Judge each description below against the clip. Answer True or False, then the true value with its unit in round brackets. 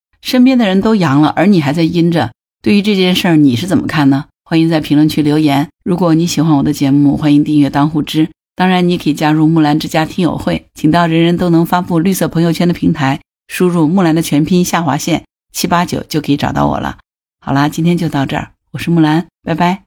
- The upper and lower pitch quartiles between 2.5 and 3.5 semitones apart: True (2.9 semitones)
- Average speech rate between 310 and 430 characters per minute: True (340 characters per minute)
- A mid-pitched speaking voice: True (160 Hz)